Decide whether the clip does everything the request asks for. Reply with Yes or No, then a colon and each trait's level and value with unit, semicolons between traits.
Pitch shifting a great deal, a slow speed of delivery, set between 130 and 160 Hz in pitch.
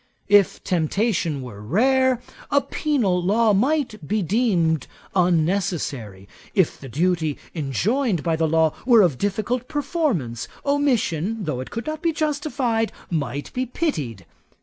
No: wide, 8.0 semitones; slow, 130 wpm; high, 195 Hz